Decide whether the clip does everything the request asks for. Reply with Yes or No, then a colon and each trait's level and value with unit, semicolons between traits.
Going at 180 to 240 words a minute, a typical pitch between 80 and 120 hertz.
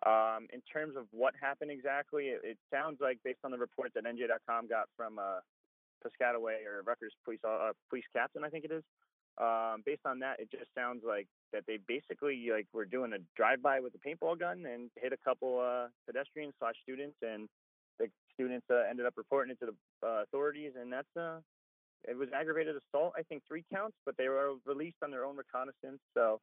No: fast, 205 wpm; low, 135 Hz